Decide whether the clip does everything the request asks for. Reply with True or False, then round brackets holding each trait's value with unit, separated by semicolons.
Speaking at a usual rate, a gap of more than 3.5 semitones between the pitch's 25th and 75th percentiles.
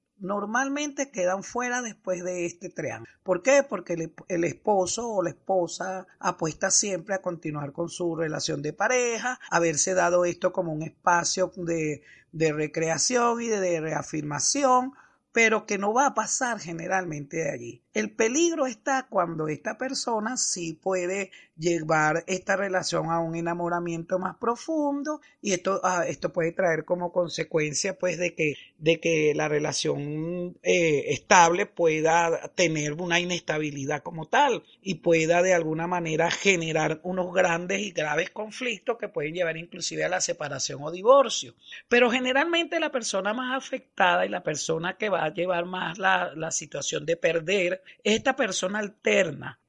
True (155 wpm; 4.6 semitones)